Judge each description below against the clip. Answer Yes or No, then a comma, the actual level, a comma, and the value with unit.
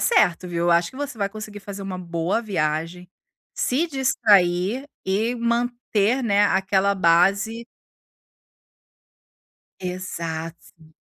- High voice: Yes, high, 195 Hz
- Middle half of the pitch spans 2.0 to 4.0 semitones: No, average, 4.8 semitones